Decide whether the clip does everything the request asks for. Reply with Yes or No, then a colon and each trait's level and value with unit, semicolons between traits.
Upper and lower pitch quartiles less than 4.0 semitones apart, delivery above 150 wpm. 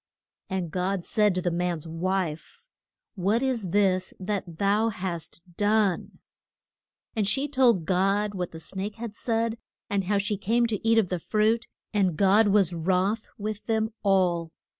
Yes: average, 3.2 semitones; average, 160 wpm